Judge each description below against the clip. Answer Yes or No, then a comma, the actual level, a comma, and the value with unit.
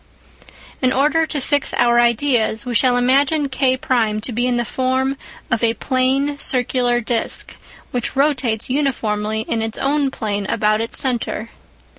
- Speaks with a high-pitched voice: Yes, very high, 250 Hz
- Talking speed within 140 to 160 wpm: Yes, average, 150 wpm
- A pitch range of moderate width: Yes, average, 3.1 semitones